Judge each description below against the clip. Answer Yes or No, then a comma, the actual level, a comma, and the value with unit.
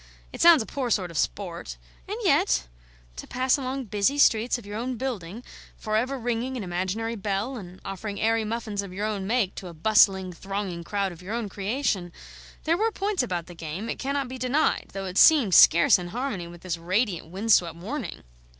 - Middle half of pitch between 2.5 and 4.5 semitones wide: No, average, 5.3 semitones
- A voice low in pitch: No, high, 210 Hz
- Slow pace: No, fast, 205 wpm